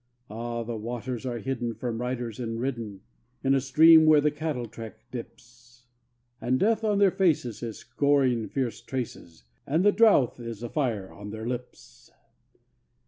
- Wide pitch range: No, average, 3.2 semitones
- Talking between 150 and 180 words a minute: Yes, average, 160 wpm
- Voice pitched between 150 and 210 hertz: No, low, 120 Hz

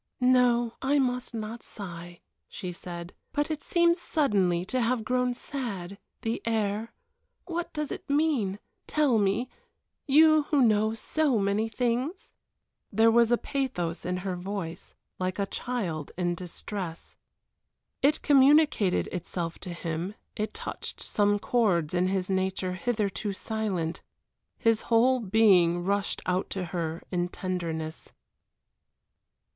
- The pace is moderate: No, slow, 130 wpm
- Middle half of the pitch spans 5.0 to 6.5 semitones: Yes, wide, 5.6 semitones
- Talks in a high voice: Yes, high, 210 Hz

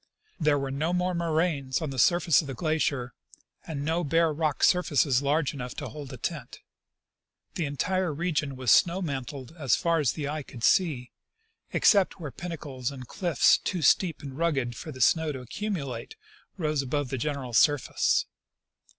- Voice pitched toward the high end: No, medium, 150 Hz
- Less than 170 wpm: No, average, 175 wpm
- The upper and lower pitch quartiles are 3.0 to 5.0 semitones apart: Yes, average, 3.8 semitones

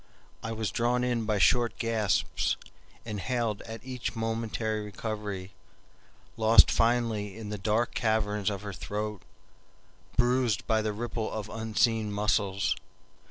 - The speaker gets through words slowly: Yes, slow, 125 wpm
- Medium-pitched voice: No, low, 110 Hz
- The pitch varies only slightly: Yes, narrow, 1.7 semitones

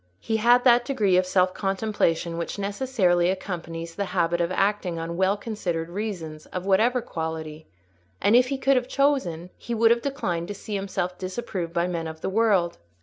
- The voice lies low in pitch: No, high, 190 Hz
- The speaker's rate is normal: Yes, average, 185 wpm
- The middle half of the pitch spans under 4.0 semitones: No, average, 4.6 semitones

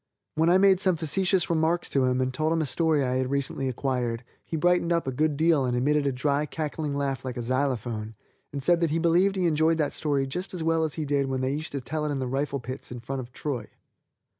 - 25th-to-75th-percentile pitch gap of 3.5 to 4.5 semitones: Yes, average, 3.9 semitones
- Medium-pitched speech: Yes, medium, 145 Hz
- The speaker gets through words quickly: Yes, fast, 255 wpm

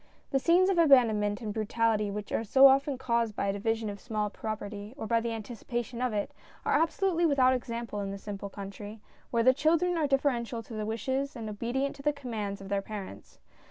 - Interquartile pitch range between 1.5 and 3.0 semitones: No, average, 4.4 semitones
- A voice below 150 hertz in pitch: No, high, 230 Hz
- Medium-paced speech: No, fast, 215 wpm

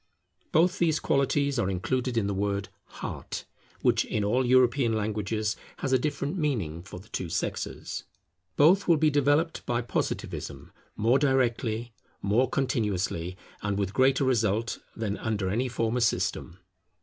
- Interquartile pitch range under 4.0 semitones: No, average, 4.9 semitones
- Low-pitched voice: Yes, low, 120 Hz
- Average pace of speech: Yes, average, 145 wpm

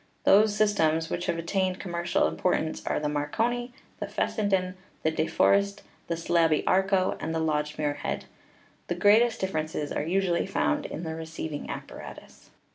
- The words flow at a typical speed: Yes, average, 165 wpm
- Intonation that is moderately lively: Yes, average, 3.7 semitones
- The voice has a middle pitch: Yes, medium, 175 Hz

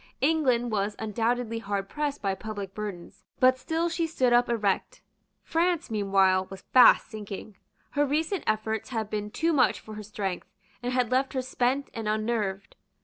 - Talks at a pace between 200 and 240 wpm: No, average, 165 wpm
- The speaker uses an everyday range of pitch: Yes, average, 4.1 semitones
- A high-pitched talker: Yes, high, 225 Hz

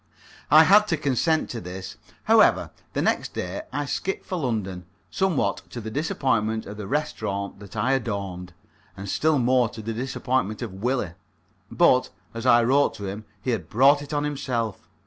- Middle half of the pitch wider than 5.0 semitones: Yes, wide, 5.6 semitones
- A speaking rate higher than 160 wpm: Yes, average, 175 wpm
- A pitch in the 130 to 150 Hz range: No, low, 120 Hz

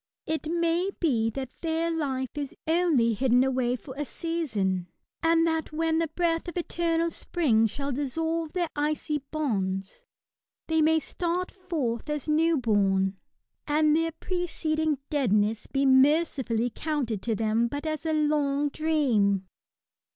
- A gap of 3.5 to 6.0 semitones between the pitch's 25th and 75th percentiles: Yes, average, 5.1 semitones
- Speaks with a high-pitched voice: Yes, very high, 300 Hz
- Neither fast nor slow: Yes, average, 155 wpm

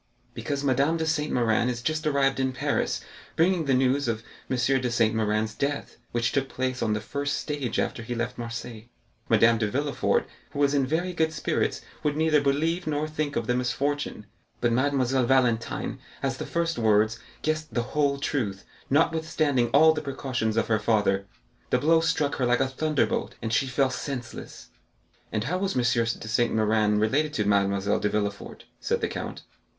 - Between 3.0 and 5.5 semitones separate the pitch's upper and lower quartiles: Yes, average, 4.3 semitones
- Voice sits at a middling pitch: No, low, 130 Hz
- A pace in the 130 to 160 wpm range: No, average, 185 wpm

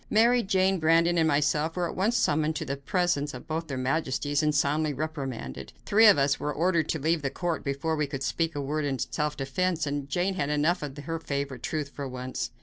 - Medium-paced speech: No, fast, 225 wpm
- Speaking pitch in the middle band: Yes, medium, 150 Hz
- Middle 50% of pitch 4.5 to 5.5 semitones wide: No, average, 3.0 semitones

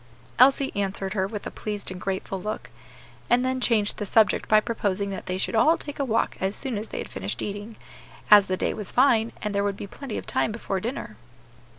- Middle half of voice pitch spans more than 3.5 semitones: No, average, 3.0 semitones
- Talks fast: Yes, fast, 225 wpm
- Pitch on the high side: Yes, high, 210 Hz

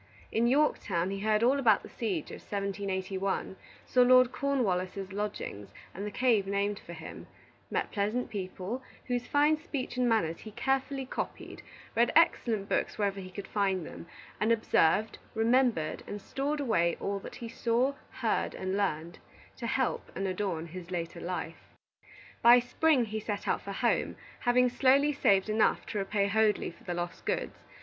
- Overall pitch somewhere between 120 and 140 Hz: No, high, 210 Hz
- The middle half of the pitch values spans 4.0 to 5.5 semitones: Yes, average, 4.5 semitones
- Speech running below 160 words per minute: No, average, 165 wpm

